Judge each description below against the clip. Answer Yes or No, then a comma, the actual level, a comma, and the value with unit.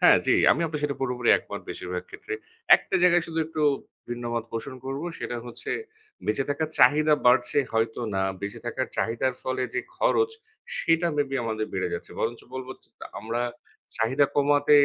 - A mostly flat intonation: No, average, 4.3 semitones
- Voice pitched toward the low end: Yes, low, 130 Hz